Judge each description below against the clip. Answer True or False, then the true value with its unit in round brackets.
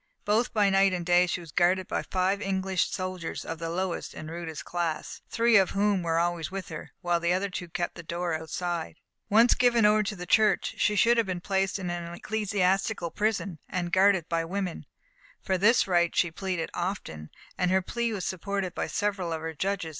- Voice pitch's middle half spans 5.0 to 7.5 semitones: False (2.6 semitones)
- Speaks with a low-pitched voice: False (185 Hz)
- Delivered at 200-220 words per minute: True (205 wpm)